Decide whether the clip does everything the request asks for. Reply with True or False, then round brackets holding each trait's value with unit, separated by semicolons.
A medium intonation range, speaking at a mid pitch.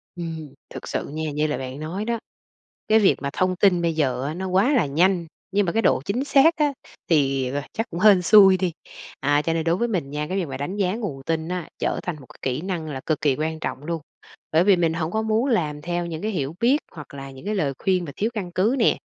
True (4.8 semitones; 170 Hz)